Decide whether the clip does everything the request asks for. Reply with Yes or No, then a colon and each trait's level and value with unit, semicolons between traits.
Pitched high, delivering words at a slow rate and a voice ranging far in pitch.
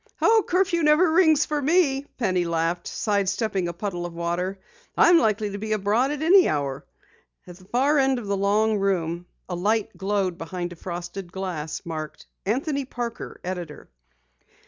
No: high, 200 Hz; average, 170 wpm; wide, 7.4 semitones